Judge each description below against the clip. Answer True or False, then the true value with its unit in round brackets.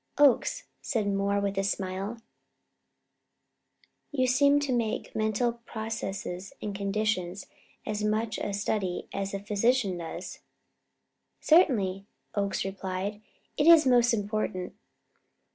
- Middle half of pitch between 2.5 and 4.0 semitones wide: True (3.2 semitones)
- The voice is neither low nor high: False (210 Hz)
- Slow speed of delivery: True (115 wpm)